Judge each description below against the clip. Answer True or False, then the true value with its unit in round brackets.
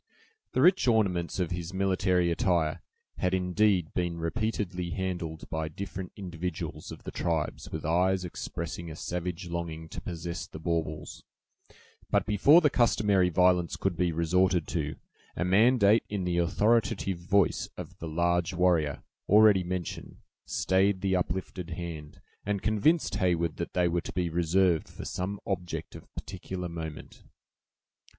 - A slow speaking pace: False (145 wpm)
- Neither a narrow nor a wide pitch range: False (2.2 semitones)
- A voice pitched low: True (90 Hz)